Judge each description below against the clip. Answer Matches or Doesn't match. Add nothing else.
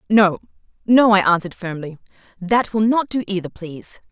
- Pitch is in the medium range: Doesn't match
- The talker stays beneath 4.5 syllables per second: Doesn't match